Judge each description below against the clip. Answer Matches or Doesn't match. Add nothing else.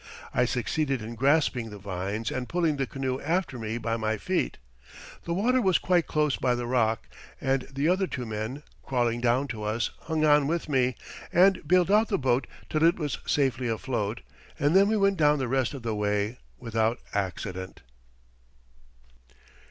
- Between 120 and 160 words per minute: Doesn't match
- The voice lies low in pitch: Matches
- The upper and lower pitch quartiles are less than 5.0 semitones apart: Doesn't match